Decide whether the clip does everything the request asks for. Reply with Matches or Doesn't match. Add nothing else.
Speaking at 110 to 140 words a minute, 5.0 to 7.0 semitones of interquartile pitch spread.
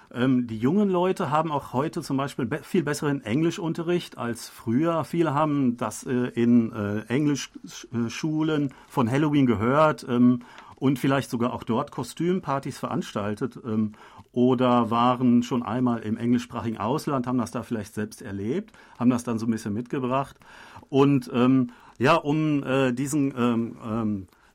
Doesn't match